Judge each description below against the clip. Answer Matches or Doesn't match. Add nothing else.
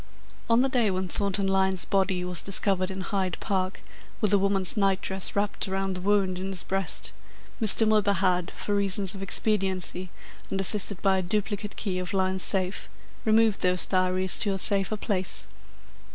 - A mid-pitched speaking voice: Doesn't match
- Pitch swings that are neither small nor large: Doesn't match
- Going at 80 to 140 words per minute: Doesn't match